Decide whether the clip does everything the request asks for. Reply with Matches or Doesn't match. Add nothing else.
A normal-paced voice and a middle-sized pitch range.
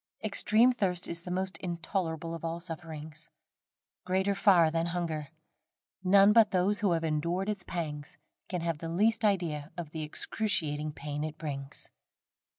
Matches